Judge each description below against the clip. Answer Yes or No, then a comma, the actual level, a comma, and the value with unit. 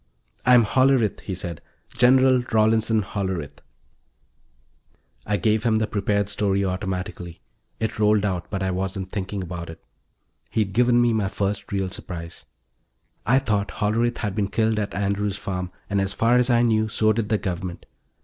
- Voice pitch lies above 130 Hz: No, low, 105 Hz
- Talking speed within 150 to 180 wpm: Yes, average, 160 wpm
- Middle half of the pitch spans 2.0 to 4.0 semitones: Yes, average, 2.7 semitones